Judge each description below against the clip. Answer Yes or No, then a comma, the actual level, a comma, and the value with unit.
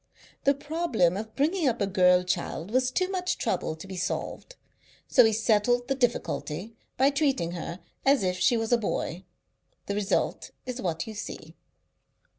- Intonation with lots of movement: Yes, wide, 6.6 semitones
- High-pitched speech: Yes, high, 225 Hz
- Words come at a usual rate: Yes, average, 170 wpm